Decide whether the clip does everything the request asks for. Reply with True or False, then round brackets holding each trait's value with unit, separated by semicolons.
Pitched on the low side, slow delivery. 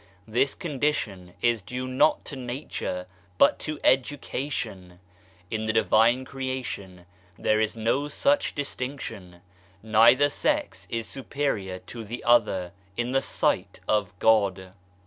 True (115 Hz; 125 wpm)